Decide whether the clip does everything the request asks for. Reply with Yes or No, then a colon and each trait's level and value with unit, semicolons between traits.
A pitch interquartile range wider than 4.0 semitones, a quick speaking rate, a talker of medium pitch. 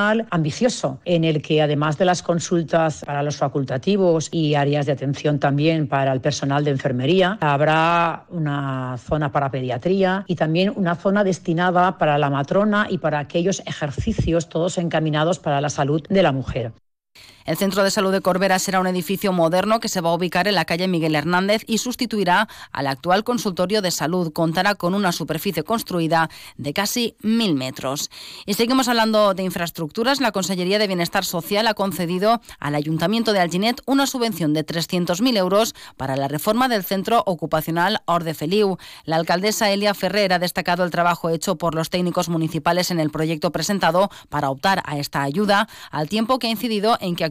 No: average, 4.4 semitones; average, 180 wpm; medium, 175 Hz